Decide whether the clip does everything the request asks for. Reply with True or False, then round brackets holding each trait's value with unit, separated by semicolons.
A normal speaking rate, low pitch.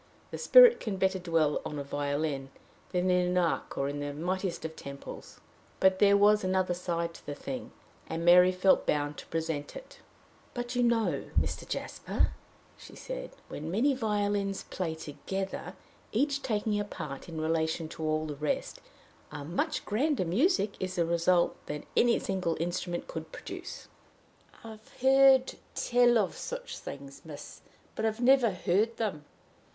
False (160 wpm; 185 Hz)